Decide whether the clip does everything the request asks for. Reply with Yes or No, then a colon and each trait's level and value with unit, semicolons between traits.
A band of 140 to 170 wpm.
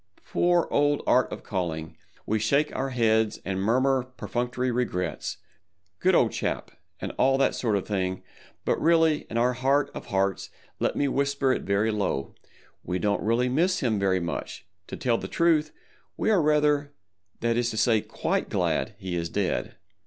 Yes: average, 165 wpm